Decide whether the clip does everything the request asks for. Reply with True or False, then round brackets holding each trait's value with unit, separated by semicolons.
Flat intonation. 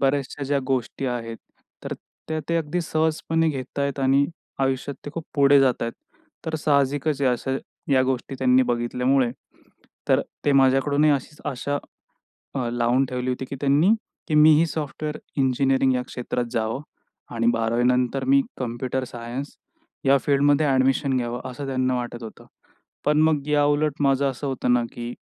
True (2.3 semitones)